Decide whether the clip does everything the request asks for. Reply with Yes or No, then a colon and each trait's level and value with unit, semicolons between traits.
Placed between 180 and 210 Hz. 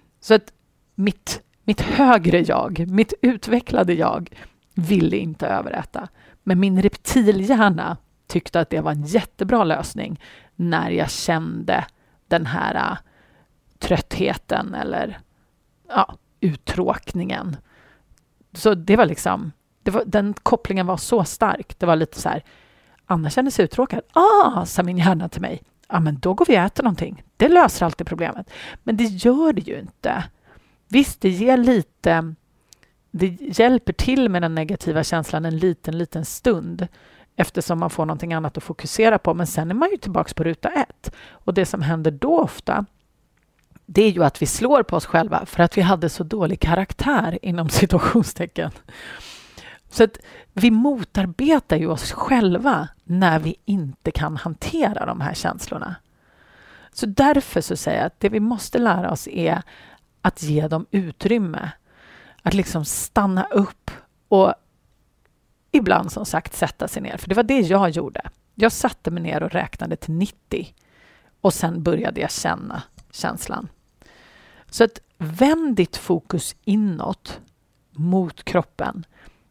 Yes: medium, 185 Hz